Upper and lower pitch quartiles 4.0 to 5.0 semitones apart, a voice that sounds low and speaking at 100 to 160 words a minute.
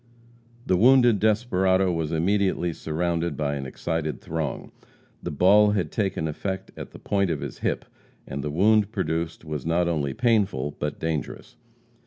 Yes: average, 4.3 semitones; very low, 85 Hz; average, 155 wpm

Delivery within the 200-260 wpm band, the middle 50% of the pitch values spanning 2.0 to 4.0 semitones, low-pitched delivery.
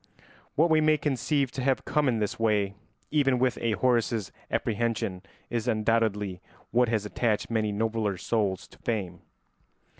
No: average, 150 wpm; average, 3.4 semitones; low, 115 Hz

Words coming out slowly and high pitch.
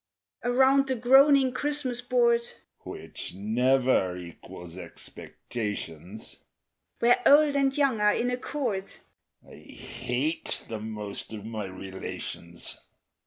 Yes: slow, 110 wpm; high, 195 Hz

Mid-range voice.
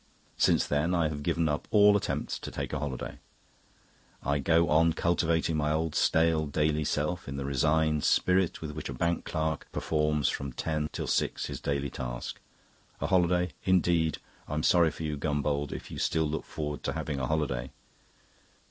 No: very low, 75 Hz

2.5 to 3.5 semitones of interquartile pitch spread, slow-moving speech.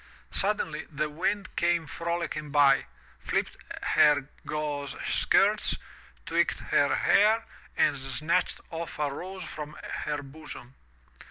Yes: average, 3.0 semitones; slow, 110 wpm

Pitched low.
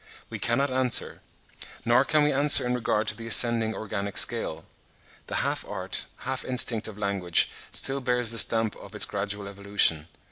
Yes: low, 115 Hz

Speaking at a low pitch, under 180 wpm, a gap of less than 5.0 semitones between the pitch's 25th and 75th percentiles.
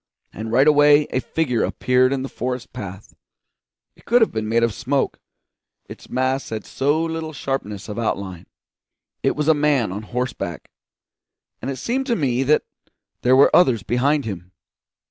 Yes: low, 130 Hz; average, 165 wpm; average, 4.6 semitones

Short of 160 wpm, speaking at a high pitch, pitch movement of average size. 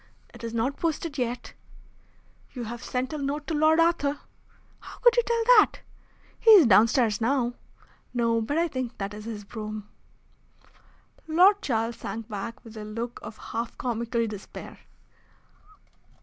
Yes: average, 150 wpm; high, 240 Hz; average, 4.9 semitones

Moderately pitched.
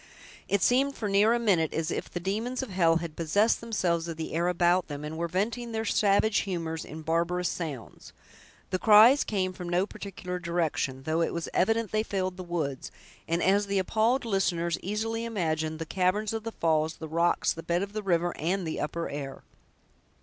Yes: medium, 180 Hz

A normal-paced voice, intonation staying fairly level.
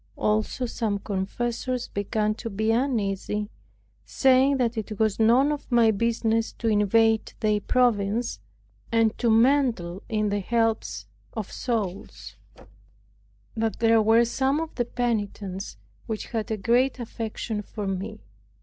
No: slow, 130 wpm; narrow, 2.3 semitones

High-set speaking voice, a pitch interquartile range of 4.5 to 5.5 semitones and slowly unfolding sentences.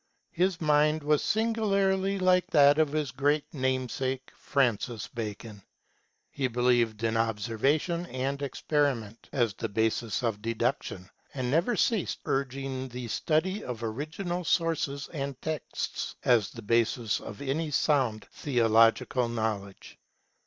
No: low, 135 Hz; average, 5.1 semitones; slow, 130 wpm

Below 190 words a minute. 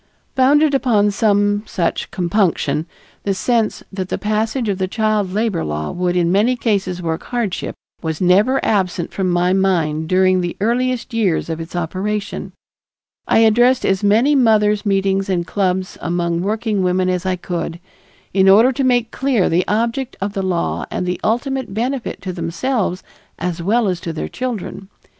Yes: average, 165 wpm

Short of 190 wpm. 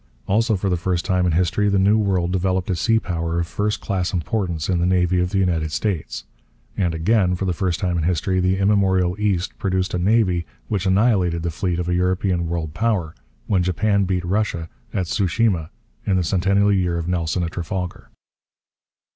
No: average, 195 wpm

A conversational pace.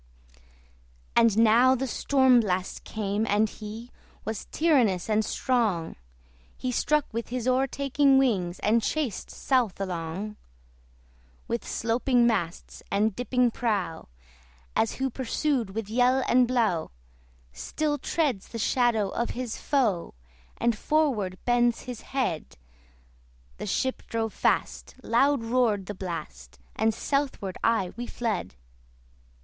No: slow, 120 wpm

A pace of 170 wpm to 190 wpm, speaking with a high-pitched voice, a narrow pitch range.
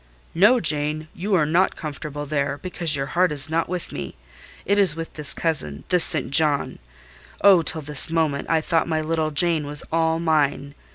No: average, 180 wpm; medium, 155 Hz; narrow, 2.2 semitones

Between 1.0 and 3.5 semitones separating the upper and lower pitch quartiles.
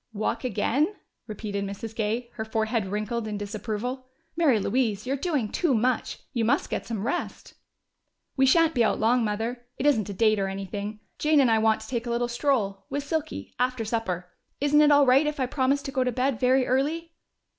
No: average, 4.0 semitones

